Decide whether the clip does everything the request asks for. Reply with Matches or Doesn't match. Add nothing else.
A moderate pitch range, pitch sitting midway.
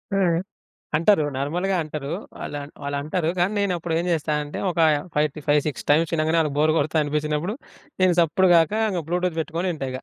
Matches